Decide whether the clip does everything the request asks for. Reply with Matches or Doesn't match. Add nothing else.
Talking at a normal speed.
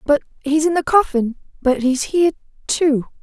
Matches